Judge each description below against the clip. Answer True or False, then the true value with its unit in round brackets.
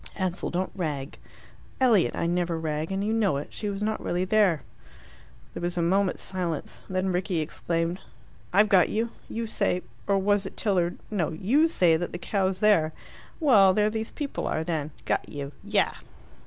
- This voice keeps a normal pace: True (180 wpm)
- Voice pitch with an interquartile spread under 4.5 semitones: True (3.5 semitones)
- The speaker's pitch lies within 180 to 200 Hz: True (185 Hz)